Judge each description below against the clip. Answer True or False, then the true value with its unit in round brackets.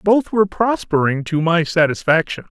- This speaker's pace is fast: False (140 wpm)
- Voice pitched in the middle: True (175 Hz)